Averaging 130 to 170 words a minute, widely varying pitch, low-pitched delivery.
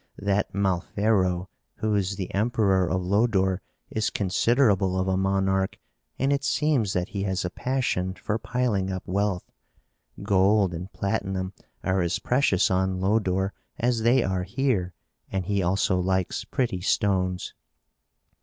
No: average, 140 wpm; narrow, 2.5 semitones; very low, 95 Hz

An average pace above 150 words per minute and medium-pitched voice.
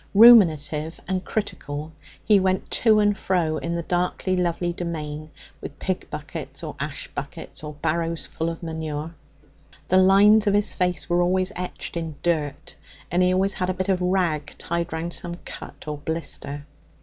Yes: average, 170 wpm; medium, 175 Hz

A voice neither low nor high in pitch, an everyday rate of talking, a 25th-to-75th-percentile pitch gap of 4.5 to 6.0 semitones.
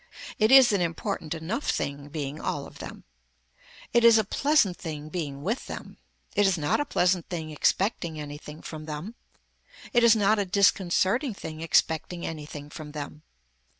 Yes: medium, 170 Hz; average, 165 wpm; average, 5.2 semitones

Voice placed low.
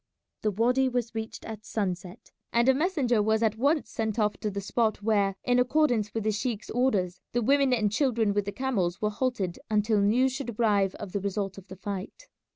No: high, 220 Hz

